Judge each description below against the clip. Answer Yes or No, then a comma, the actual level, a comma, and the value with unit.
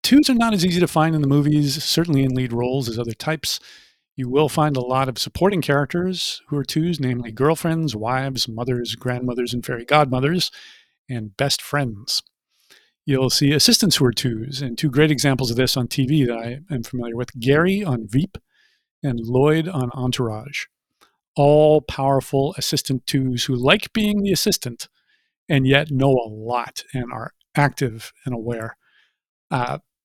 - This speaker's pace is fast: No, average, 170 wpm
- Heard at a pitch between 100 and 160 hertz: Yes, medium, 140 Hz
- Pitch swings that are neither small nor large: Yes, average, 3.8 semitones